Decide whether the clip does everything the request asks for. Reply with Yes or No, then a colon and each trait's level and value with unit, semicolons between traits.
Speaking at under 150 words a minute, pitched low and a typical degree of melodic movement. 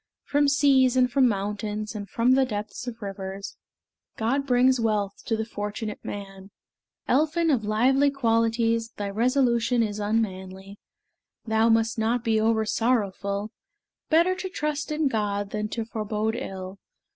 No: average, 140 wpm; high, 225 Hz; average, 3.6 semitones